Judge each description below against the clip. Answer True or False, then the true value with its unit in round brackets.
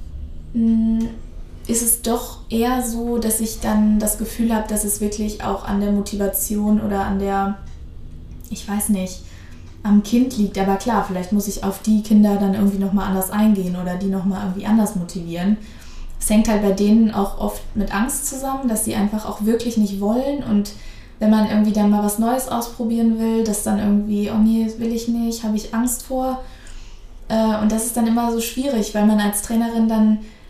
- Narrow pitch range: True (2.3 semitones)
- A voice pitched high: True (215 Hz)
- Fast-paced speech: True (195 wpm)